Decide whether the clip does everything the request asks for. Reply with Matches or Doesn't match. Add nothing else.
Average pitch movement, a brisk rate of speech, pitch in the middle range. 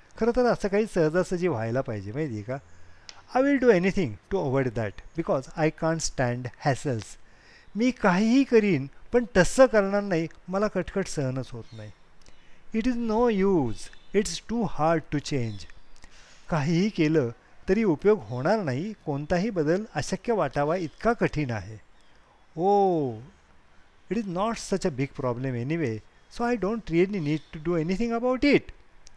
Doesn't match